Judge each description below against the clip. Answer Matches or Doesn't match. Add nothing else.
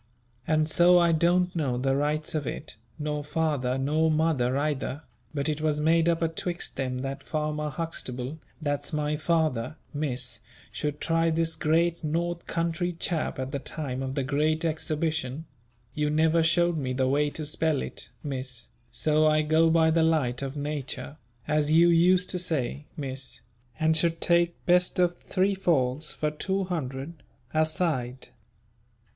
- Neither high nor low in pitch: Matches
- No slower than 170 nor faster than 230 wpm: Doesn't match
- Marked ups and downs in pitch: Doesn't match